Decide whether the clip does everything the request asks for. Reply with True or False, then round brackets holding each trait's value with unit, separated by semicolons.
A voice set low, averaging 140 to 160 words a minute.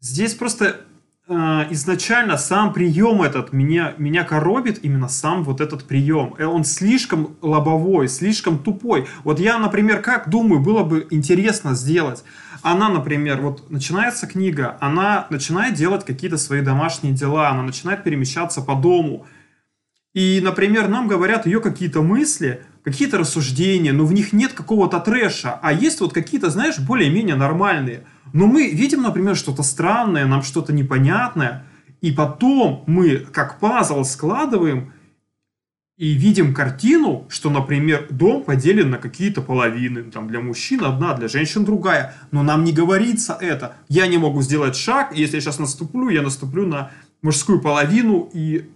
False (165 Hz; 150 wpm)